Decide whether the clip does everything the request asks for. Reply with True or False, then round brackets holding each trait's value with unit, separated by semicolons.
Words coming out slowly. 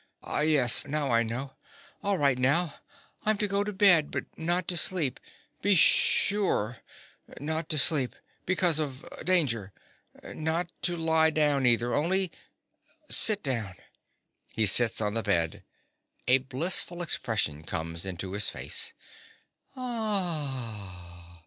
True (125 wpm)